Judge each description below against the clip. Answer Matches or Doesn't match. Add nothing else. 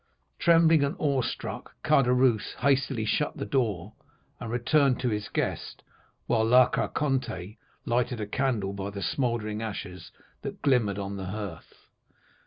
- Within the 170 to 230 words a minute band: Doesn't match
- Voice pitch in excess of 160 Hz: Doesn't match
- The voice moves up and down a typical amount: Matches